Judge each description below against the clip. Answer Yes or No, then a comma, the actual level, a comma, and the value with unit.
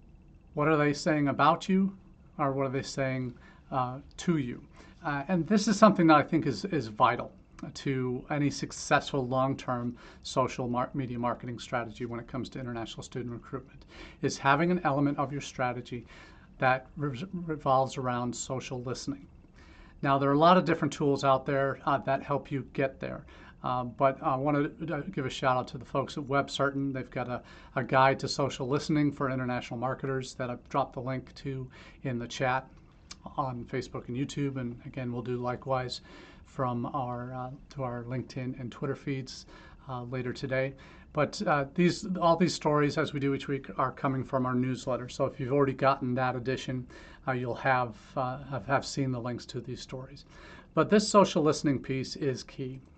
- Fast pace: No, average, 190 wpm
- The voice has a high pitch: No, low, 135 Hz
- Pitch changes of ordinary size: No, narrow, 2.3 semitones